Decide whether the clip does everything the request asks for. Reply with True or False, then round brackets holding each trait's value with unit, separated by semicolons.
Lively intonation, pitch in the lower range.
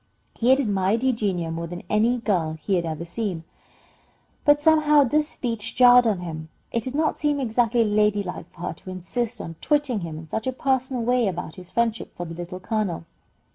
False (6.0 semitones; 215 Hz)